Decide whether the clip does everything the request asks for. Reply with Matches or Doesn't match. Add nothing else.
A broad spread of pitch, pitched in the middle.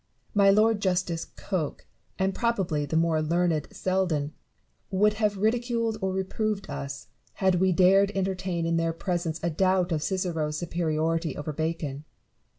Doesn't match